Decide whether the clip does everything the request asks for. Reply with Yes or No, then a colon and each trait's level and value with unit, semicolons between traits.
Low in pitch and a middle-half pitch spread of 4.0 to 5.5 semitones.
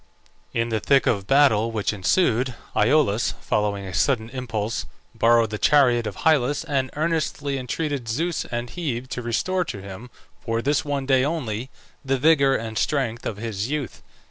Yes: low, 125 Hz; average, 4.3 semitones